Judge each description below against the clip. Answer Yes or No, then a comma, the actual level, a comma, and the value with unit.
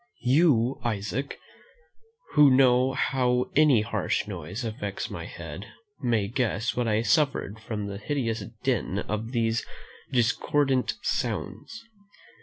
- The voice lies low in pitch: Yes, low, 120 Hz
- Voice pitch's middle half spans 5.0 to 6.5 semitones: No, average, 3.7 semitones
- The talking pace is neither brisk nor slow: No, slow, 115 wpm